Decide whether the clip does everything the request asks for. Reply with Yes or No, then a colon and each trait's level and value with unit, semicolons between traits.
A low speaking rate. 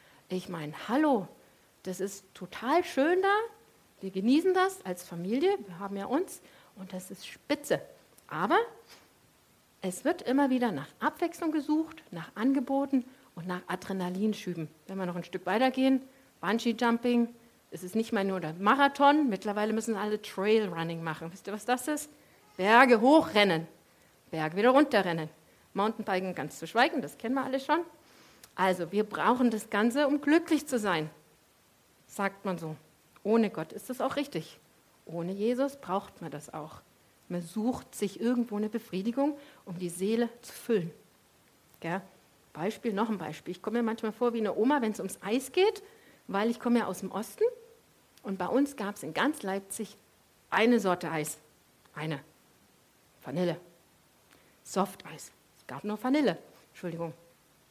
No: average, 160 wpm